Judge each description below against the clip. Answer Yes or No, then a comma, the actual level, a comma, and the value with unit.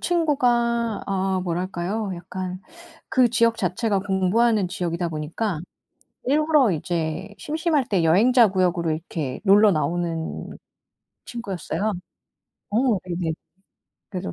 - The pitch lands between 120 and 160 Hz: No, high, 190 Hz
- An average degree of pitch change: Yes, average, 5.0 semitones